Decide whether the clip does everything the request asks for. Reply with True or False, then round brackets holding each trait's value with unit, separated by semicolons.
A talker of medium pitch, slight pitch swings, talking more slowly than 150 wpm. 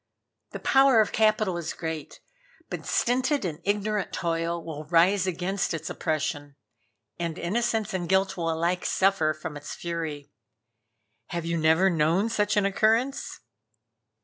False (175 Hz; 4.2 semitones; 140 wpm)